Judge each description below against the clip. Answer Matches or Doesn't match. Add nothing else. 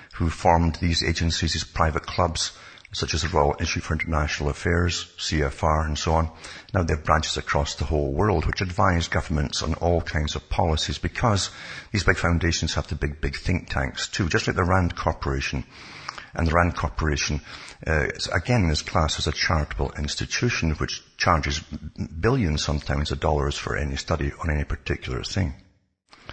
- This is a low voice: Matches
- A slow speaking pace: Doesn't match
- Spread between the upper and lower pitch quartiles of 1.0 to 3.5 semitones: Matches